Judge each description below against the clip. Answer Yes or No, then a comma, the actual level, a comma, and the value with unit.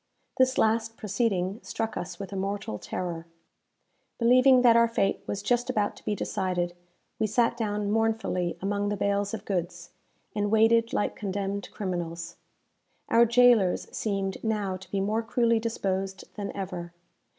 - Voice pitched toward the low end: No, high, 205 Hz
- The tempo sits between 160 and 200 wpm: No, average, 150 wpm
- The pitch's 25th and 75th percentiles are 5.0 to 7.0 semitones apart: No, average, 2.9 semitones